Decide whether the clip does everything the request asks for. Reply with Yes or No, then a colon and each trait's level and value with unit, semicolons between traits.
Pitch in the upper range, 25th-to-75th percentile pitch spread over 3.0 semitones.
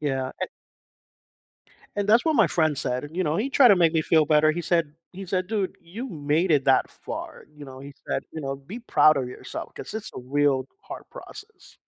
No: medium, 160 Hz; wide, 5.4 semitones